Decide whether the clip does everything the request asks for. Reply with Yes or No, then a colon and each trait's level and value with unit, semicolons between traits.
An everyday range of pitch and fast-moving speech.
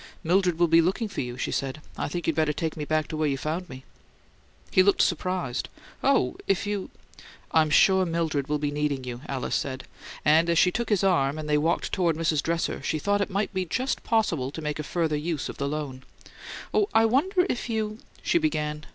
Yes: average, 4.3 semitones; fast, 225 wpm